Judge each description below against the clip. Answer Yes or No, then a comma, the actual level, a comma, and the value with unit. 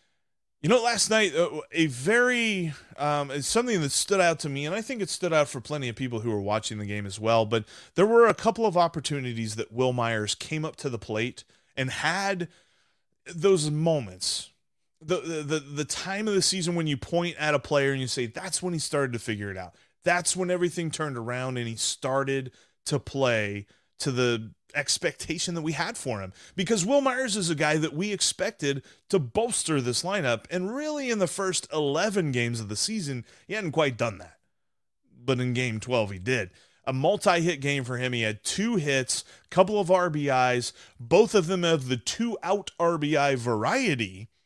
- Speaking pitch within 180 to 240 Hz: No, medium, 150 Hz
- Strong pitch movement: Yes, wide, 6.7 semitones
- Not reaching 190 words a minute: No, average, 200 wpm